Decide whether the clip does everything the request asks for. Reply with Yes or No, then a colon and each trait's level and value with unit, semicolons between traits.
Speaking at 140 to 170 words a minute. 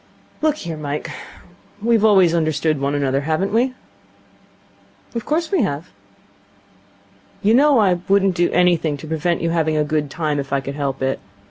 Yes: average, 165 wpm